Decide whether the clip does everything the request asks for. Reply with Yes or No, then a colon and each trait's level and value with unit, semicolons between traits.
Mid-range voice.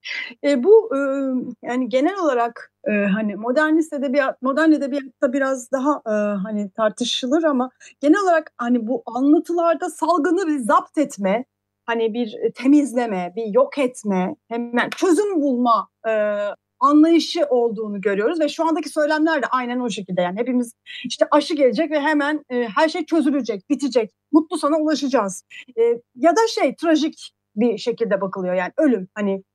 No: very high, 265 Hz